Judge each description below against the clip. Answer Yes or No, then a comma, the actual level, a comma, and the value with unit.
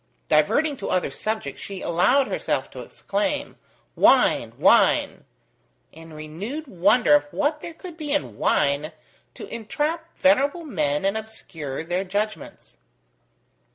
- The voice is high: Yes, high, 215 Hz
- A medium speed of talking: No, slow, 125 wpm